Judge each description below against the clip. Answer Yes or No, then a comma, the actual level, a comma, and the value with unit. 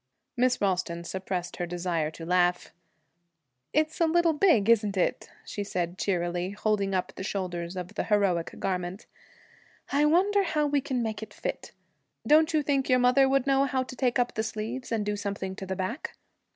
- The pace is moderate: Yes, average, 185 wpm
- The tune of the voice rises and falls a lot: Yes, wide, 6.7 semitones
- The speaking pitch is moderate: No, high, 210 Hz